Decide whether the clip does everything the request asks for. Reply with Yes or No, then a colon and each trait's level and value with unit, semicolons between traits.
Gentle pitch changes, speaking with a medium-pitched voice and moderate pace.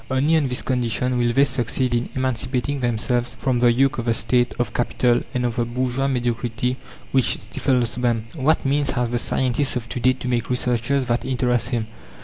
No: narrow, 1.5 semitones; low, 125 Hz; average, 195 wpm